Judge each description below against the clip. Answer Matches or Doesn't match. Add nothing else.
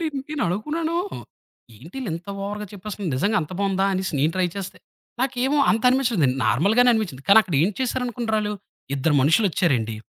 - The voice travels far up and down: Matches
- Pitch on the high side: Matches